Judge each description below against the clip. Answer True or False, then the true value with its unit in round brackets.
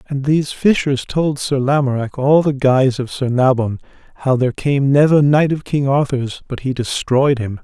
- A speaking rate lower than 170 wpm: False (190 wpm)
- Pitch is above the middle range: False (135 Hz)